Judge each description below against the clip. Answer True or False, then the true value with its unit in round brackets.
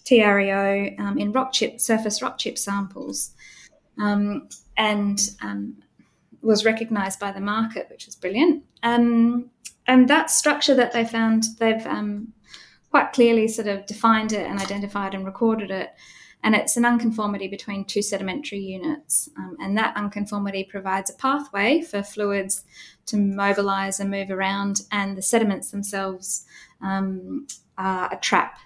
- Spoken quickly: False (145 wpm)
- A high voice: True (205 Hz)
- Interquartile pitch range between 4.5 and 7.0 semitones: False (2.7 semitones)